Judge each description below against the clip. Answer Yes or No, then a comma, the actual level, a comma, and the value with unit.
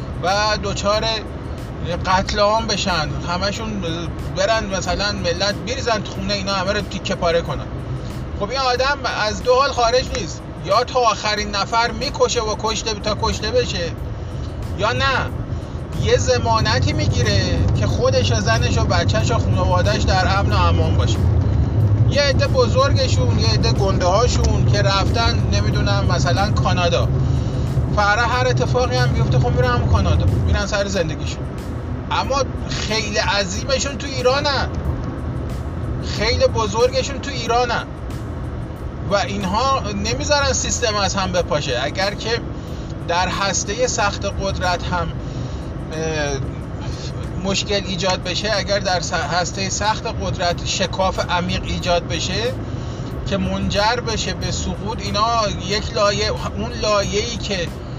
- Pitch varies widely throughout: No, average, 4.4 semitones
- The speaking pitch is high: No, low, 110 Hz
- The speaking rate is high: No, average, 130 wpm